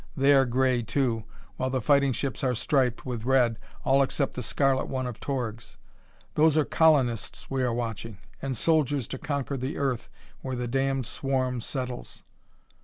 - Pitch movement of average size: No, narrow, 2.0 semitones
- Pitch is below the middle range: Yes, low, 130 Hz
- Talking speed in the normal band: Yes, average, 170 wpm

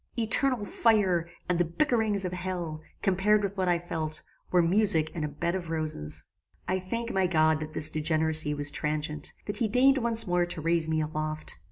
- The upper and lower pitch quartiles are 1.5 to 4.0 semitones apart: No, average, 4.4 semitones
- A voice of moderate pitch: Yes, medium, 175 Hz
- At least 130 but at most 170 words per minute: No, average, 190 wpm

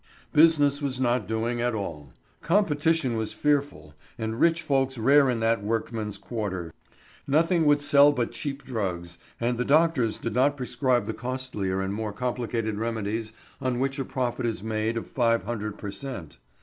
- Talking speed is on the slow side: No, average, 165 wpm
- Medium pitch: No, low, 120 Hz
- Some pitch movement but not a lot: Yes, average, 4.1 semitones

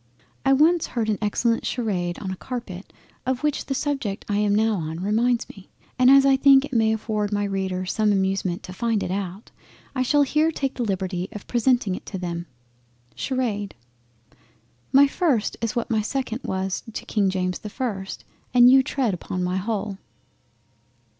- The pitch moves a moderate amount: Yes, average, 4.9 semitones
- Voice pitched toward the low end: No, high, 215 Hz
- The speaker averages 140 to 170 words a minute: No, average, 180 wpm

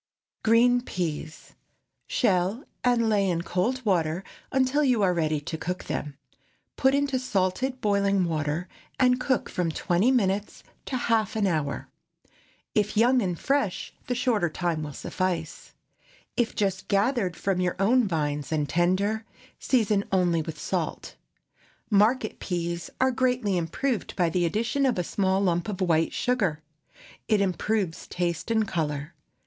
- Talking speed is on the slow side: No, average, 145 wpm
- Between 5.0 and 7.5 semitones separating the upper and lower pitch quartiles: Yes, wide, 5.5 semitones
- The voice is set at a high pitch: Yes, high, 195 Hz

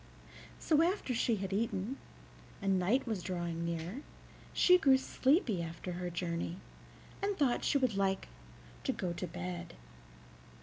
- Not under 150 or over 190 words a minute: No, average, 140 wpm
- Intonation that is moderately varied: No, wide, 7.2 semitones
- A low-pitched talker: No, high, 195 Hz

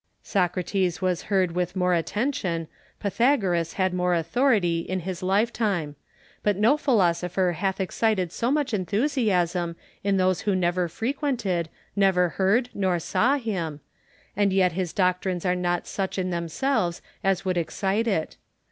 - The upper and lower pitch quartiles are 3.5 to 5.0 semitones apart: No, average, 2.9 semitones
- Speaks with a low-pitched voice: No, medium, 185 Hz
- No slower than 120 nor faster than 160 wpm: Yes, average, 140 wpm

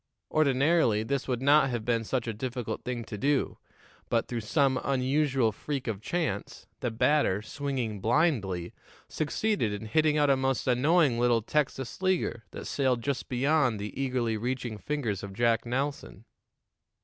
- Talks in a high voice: No, low, 125 Hz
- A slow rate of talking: No, average, 155 wpm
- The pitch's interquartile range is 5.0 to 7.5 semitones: No, average, 3.9 semitones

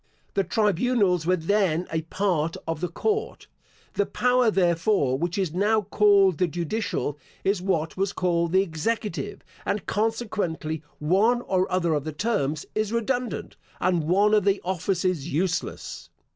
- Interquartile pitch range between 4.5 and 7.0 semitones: No, average, 4.1 semitones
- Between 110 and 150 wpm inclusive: Yes, average, 145 wpm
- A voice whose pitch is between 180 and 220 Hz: Yes, medium, 185 Hz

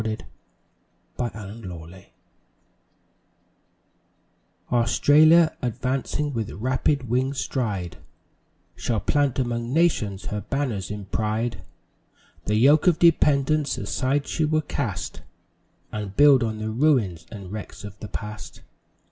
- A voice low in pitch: Yes, low, 120 Hz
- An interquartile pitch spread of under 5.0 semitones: No, average, 5.3 semitones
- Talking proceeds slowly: Yes, slow, 110 wpm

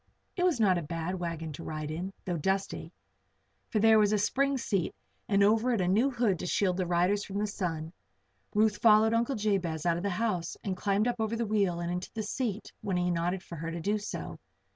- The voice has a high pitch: Yes, high, 195 Hz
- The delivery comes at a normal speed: No, fast, 230 wpm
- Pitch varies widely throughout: No, average, 3.8 semitones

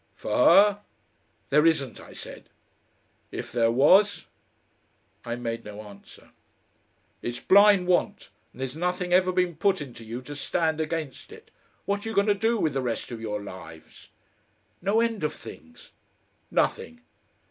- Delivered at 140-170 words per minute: Yes, average, 155 wpm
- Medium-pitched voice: Yes, medium, 160 Hz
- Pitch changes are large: Yes, wide, 8.6 semitones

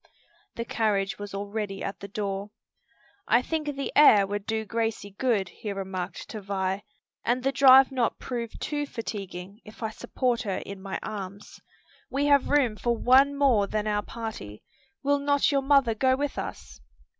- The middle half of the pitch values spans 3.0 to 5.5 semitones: Yes, average, 4.8 semitones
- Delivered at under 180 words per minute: Yes, average, 170 wpm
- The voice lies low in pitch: No, high, 220 Hz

